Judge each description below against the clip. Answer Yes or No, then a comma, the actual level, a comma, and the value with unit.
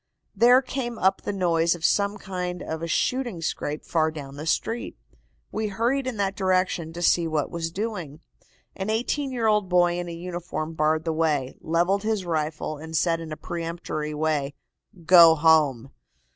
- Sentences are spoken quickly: No, average, 175 wpm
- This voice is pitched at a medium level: Yes, medium, 170 Hz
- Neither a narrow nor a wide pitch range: Yes, average, 4.0 semitones